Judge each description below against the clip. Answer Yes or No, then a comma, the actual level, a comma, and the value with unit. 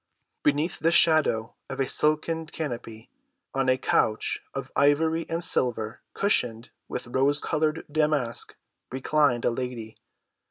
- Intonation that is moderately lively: Yes, average, 4.6 semitones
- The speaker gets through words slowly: Yes, slow, 120 wpm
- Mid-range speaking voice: Yes, medium, 145 Hz